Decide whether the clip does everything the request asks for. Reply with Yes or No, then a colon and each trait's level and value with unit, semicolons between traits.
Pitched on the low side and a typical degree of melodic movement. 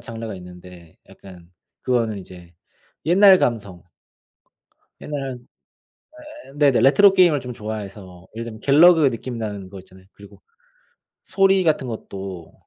No: low, 110 Hz; wide, 7.0 semitones